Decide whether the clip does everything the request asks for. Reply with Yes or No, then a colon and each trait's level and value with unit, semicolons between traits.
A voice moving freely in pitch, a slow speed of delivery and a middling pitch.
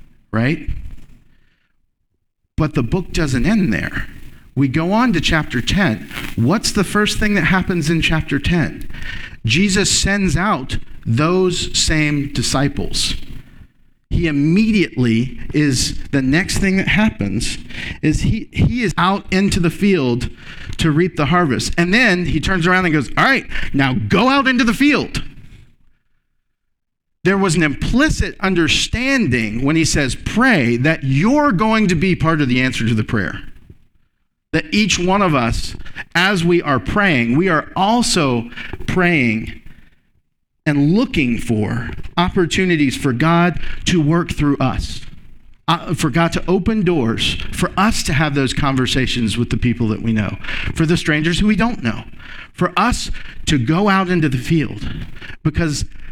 No: wide, 7.6 semitones; average, 150 wpm; medium, 155 Hz